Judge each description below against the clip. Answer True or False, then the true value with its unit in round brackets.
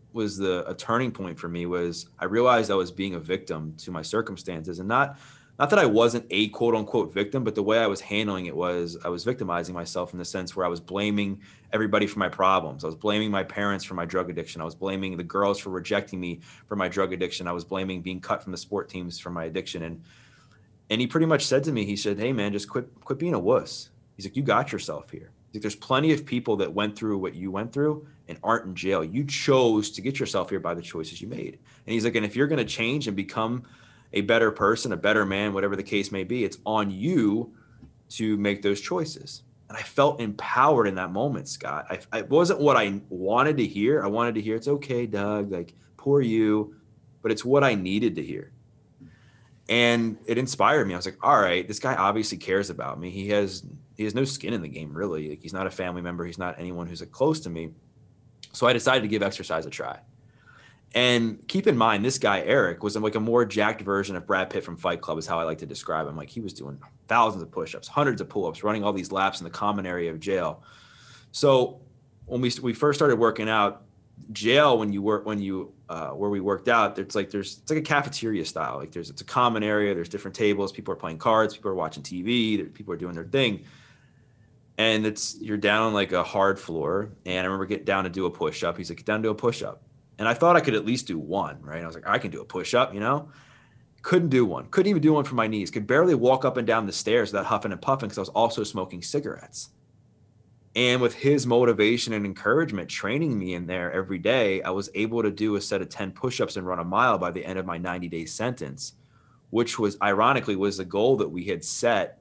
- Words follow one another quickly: True (245 wpm)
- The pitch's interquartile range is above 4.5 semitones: False (4.0 semitones)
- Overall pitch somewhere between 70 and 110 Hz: True (105 Hz)